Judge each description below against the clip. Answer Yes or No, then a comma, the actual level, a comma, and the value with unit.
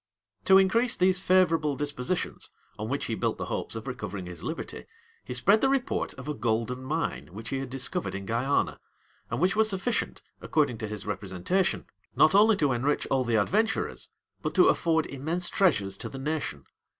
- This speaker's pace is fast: No, average, 185 wpm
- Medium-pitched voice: Yes, medium, 145 Hz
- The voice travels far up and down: Yes, wide, 8.6 semitones